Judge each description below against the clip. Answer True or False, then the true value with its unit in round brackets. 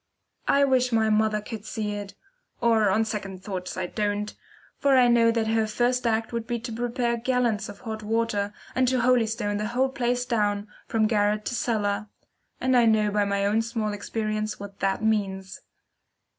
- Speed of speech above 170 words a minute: True (185 wpm)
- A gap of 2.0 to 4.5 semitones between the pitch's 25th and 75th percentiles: True (2.4 semitones)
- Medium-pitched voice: False (220 Hz)